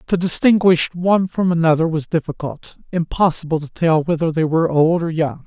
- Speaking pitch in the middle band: Yes, medium, 165 Hz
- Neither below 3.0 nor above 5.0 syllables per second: No, 5.4 syllables/s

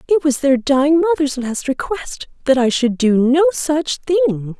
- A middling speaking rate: Yes, average, 185 wpm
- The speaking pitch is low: No, very high, 270 Hz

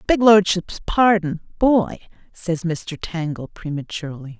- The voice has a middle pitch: Yes, medium, 180 Hz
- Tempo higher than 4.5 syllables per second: No, 4.3 syllables/s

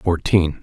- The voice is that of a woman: No, male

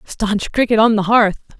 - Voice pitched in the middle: No, high, 215 Hz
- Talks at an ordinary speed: Yes, average, 190 wpm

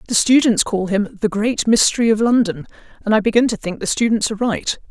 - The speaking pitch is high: Yes, high, 215 Hz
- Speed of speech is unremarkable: No, fast, 220 wpm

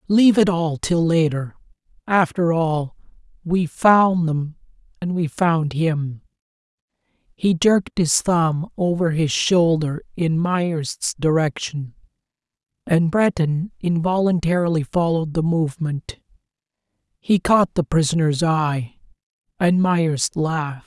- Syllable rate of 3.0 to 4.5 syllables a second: Yes, 3.9 syllables/s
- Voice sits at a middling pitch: Yes, medium, 165 Hz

